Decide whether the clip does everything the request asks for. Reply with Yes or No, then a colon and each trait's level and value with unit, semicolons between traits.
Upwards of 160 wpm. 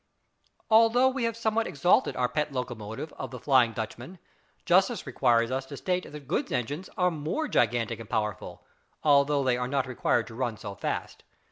Yes: average, 175 wpm